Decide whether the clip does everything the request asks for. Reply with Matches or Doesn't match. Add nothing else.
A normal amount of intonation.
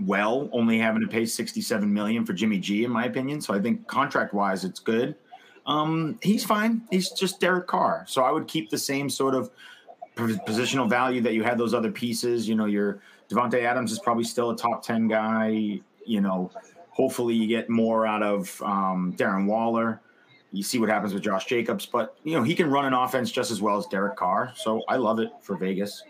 Doesn't match